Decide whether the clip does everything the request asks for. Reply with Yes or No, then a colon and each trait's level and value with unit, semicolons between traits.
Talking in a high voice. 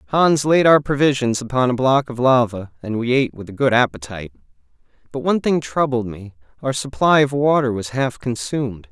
No: low, 130 Hz